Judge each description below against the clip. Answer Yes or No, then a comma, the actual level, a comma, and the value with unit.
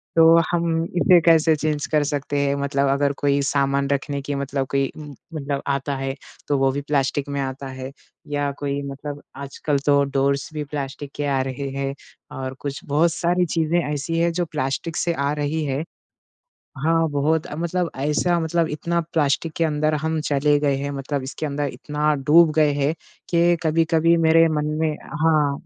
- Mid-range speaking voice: Yes, medium, 145 Hz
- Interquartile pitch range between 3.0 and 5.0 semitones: No, narrow, 2.5 semitones